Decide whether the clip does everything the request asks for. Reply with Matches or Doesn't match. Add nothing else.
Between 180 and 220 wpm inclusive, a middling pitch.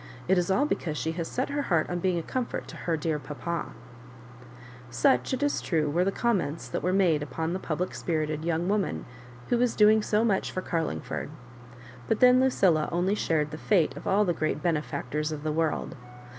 Matches